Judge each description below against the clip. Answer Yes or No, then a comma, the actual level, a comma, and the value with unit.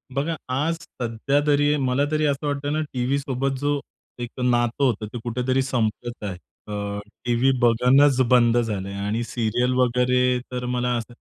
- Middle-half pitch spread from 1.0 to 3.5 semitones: Yes, average, 2.8 semitones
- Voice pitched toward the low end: Yes, low, 125 Hz